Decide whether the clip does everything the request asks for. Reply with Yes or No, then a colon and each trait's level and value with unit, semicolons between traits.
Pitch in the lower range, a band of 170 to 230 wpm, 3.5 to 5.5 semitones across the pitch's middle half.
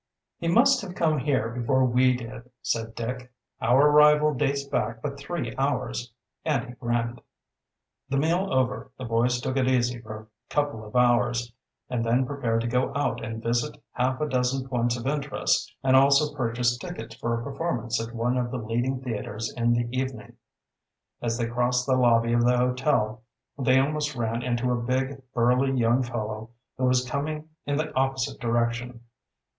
No: low, 125 Hz; average, 175 wpm; narrow, 2.4 semitones